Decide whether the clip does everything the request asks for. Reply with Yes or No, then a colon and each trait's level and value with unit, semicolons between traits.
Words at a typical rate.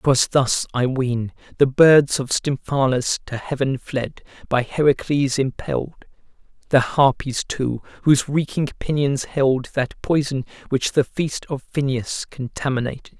No: slow, 130 wpm